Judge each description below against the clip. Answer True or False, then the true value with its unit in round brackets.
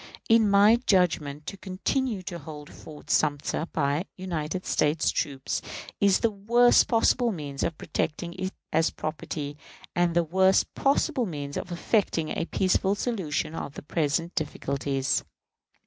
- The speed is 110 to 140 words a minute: True (135 wpm)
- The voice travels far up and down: False (4.8 semitones)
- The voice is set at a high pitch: False (170 Hz)